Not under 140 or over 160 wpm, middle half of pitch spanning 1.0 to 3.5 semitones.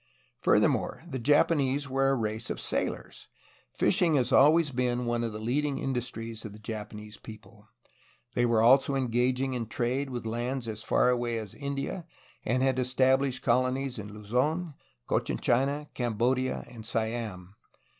Yes: average, 155 wpm; average, 3.0 semitones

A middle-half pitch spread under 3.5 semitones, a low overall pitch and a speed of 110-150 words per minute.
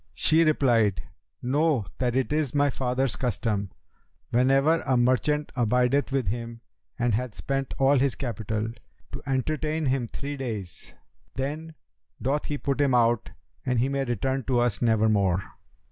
Yes: average, 3.1 semitones; low, 130 Hz; average, 145 wpm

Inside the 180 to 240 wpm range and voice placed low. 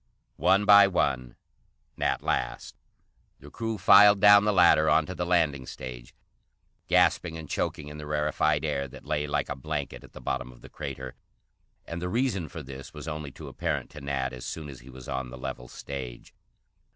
Yes: average, 190 wpm; very low, 75 Hz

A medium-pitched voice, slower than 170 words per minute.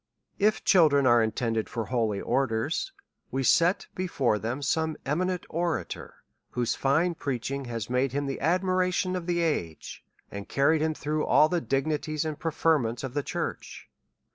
Yes: medium, 145 Hz; average, 160 wpm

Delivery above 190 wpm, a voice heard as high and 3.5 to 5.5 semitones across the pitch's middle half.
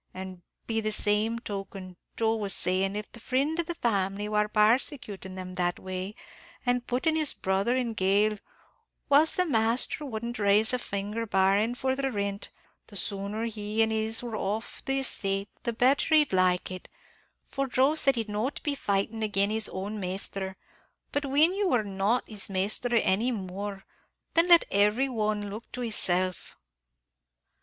No: average, 165 wpm; high, 215 Hz; average, 4.0 semitones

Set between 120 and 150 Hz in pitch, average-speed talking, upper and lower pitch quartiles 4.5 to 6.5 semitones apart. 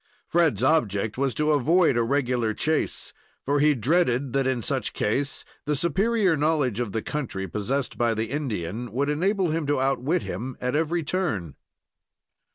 Yes: medium, 140 Hz; average, 165 wpm; average, 4.8 semitones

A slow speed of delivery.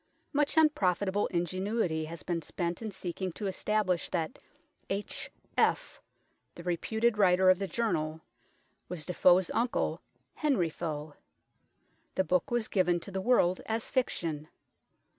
Yes: slow, 130 wpm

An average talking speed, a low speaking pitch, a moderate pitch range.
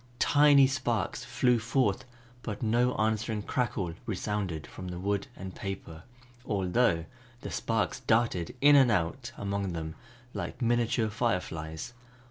No: slow, 125 wpm; low, 105 Hz; average, 4.6 semitones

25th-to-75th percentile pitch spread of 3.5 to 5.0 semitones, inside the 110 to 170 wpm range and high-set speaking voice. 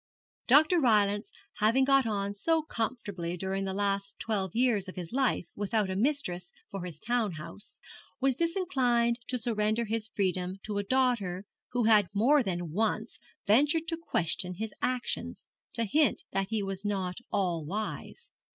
Yes: average, 4.4 semitones; average, 160 wpm; high, 215 Hz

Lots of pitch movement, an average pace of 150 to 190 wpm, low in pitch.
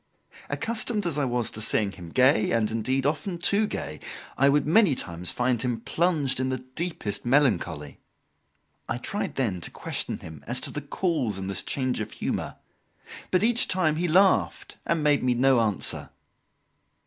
Yes: wide, 6.7 semitones; average, 170 wpm; low, 130 Hz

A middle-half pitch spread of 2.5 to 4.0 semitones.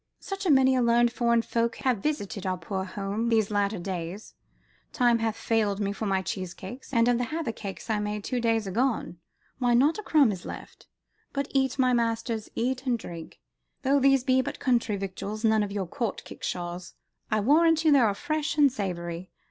No: average, 4.6 semitones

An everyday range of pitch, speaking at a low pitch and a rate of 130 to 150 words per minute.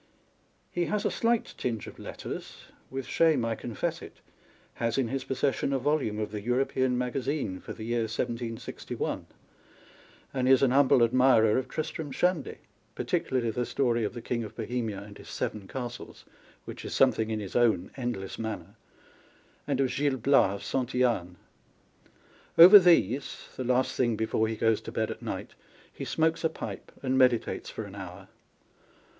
No: average, 3.3 semitones; low, 125 Hz; average, 170 wpm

